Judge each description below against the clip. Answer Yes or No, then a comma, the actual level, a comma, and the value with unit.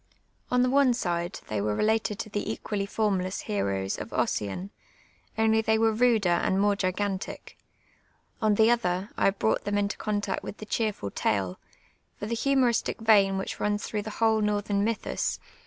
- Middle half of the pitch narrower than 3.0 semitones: Yes, narrow, 2.6 semitones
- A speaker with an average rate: Yes, average, 185 wpm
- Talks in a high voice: Yes, high, 205 Hz